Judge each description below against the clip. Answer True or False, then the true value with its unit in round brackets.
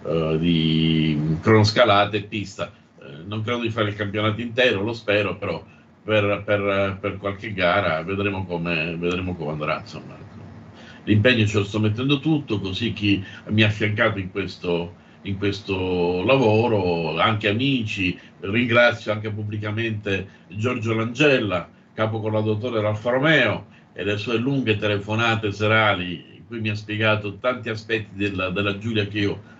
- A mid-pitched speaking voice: False (105 Hz)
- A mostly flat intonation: True (2.1 semitones)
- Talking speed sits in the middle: True (150 wpm)